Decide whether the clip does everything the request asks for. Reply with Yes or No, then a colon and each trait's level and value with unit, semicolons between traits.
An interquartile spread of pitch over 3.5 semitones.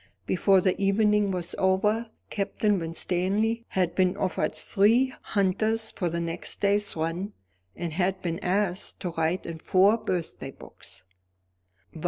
No: average, 2.8 semitones